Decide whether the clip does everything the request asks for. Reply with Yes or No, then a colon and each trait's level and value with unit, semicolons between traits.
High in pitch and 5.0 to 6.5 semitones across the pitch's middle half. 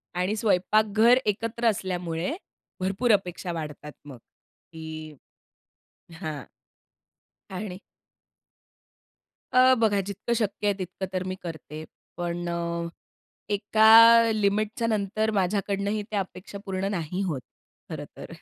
No: high, 195 Hz; average, 3.7 semitones